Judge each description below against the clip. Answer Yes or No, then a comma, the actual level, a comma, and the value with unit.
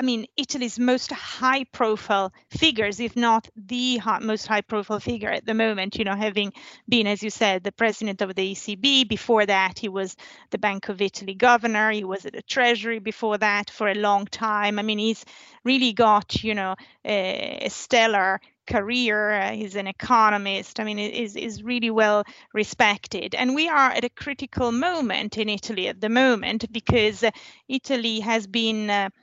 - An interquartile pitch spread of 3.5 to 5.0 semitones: No, average, 2.7 semitones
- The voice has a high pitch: Yes, high, 220 Hz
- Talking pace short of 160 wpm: No, average, 175 wpm